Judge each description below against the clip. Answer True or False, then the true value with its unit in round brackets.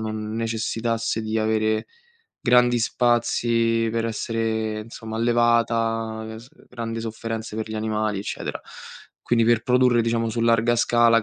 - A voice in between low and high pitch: False (115 Hz)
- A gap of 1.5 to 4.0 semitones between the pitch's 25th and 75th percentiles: False (1.0 semitones)